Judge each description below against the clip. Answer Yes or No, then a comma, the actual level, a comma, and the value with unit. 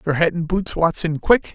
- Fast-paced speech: Yes, fast, 235 wpm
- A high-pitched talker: No, medium, 165 Hz